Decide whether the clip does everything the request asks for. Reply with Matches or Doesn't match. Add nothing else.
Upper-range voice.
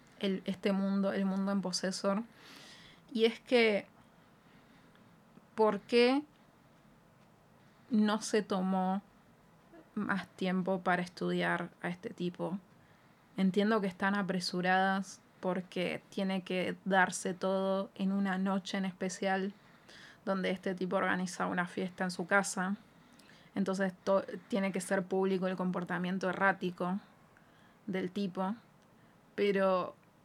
Matches